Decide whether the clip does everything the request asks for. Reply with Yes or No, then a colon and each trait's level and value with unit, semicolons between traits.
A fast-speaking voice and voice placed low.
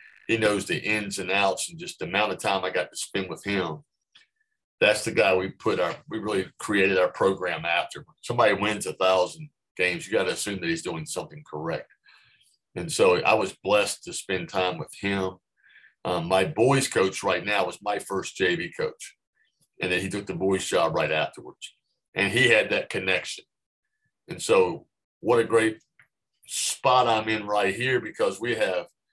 No: average, 190 wpm; low, 110 Hz